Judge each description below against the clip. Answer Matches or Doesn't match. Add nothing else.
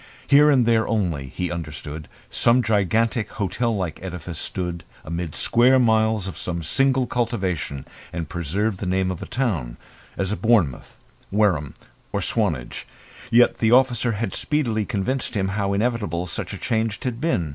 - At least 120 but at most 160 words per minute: Matches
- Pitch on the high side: Doesn't match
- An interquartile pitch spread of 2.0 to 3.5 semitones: Doesn't match